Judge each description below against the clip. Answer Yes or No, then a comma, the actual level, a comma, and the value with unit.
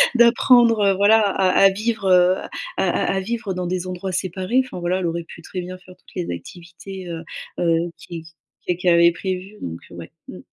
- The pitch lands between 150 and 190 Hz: Yes, medium, 185 Hz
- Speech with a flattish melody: Yes, narrow, 2.2 semitones